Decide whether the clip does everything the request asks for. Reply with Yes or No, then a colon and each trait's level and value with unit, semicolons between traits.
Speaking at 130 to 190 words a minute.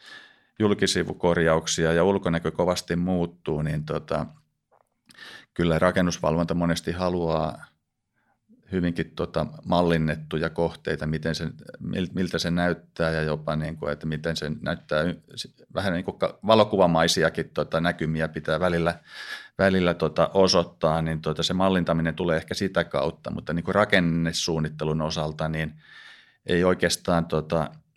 No: average, 120 wpm